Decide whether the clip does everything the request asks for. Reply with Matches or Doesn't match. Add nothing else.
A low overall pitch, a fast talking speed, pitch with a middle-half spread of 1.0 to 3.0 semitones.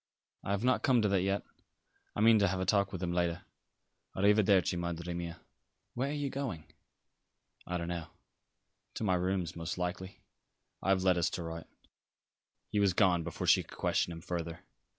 Doesn't match